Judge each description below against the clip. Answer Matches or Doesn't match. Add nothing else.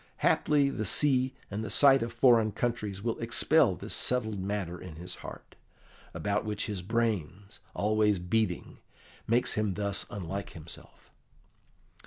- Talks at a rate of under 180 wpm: Matches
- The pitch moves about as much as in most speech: Matches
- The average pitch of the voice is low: Matches